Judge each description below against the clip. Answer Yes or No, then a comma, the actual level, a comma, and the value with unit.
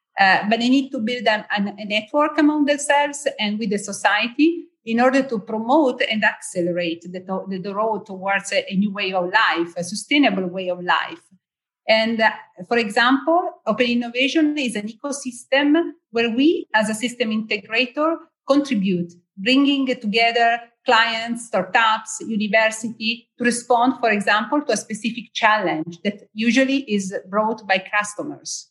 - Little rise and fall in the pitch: No, average, 4.1 semitones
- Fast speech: No, average, 155 wpm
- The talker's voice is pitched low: No, high, 225 Hz